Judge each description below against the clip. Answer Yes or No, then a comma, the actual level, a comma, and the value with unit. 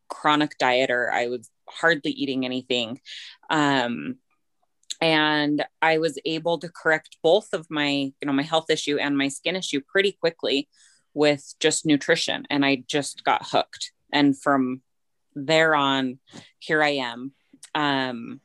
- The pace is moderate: Yes, average, 145 wpm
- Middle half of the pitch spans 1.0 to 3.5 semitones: Yes, average, 2.8 semitones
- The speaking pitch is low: No, medium, 145 Hz